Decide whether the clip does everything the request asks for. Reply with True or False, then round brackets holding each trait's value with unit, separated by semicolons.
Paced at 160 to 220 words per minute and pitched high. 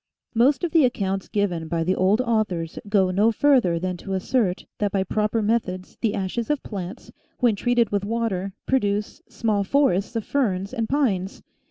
True (180 wpm; 205 Hz)